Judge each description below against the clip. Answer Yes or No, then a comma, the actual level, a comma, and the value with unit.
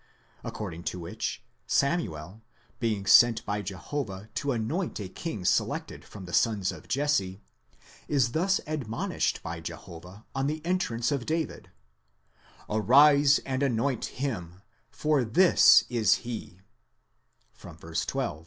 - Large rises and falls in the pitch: Yes, wide, 7.0 semitones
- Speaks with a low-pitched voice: Yes, low, 115 Hz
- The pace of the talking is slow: Yes, slow, 125 wpm